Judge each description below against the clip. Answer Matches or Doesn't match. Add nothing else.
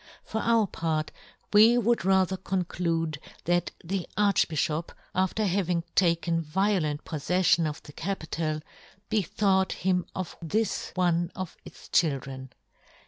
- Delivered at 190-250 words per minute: Doesn't match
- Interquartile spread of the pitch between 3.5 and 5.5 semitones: Doesn't match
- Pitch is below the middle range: Doesn't match